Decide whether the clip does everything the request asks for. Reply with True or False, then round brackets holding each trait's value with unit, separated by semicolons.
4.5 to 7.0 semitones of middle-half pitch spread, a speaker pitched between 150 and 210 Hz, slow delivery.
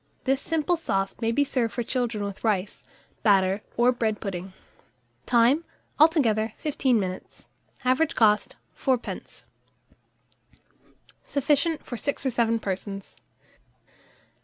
False (4.8 semitones; 235 Hz; 110 wpm)